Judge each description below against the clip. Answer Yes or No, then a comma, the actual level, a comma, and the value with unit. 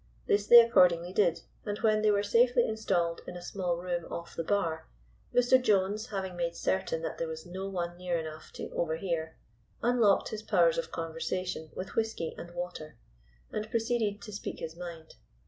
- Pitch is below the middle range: No, medium, 185 Hz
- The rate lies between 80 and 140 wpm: No, average, 180 wpm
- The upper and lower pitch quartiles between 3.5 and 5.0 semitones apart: Yes, average, 4.1 semitones